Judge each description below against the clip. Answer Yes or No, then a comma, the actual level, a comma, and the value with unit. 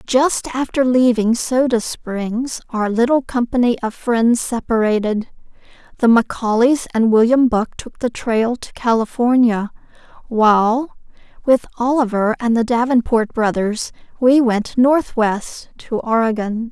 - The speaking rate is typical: No, slow, 120 wpm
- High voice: Yes, high, 235 Hz